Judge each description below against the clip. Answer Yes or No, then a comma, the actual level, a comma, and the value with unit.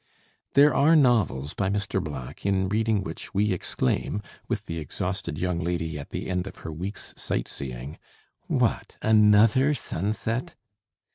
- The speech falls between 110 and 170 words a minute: Yes, average, 145 wpm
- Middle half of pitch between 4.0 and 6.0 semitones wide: Yes, average, 5.1 semitones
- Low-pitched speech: Yes, very low, 95 Hz